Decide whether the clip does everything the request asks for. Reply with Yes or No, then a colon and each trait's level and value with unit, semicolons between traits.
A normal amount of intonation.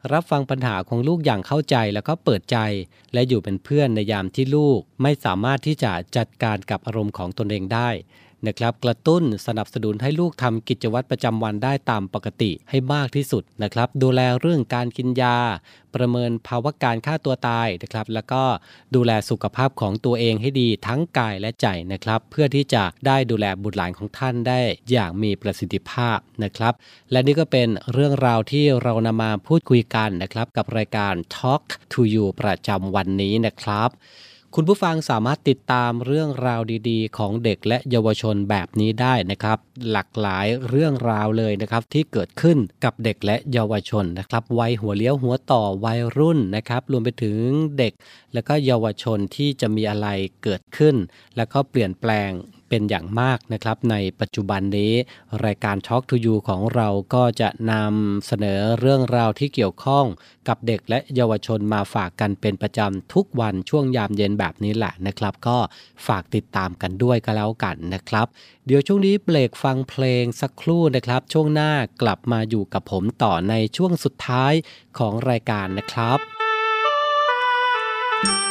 Yes: average, 3.8 semitones